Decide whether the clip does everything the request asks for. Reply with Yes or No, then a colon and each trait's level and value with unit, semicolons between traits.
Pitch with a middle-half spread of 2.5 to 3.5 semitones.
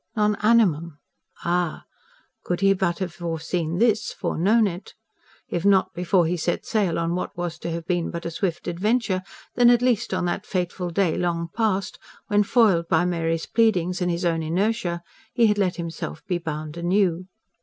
Yes: average, 3.1 semitones